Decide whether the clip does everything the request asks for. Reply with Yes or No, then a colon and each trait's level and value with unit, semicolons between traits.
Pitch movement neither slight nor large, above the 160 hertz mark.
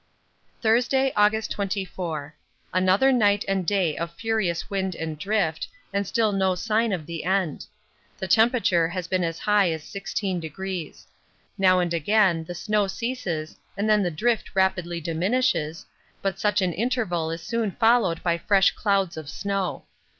Yes: average, 3.8 semitones; high, 190 Hz